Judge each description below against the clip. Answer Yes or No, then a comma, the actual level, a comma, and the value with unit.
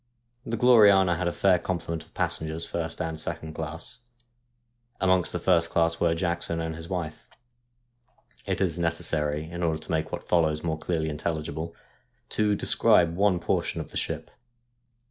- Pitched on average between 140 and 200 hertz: No, very low, 85 Hz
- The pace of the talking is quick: No, average, 160 wpm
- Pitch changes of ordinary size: No, narrow, 2.0 semitones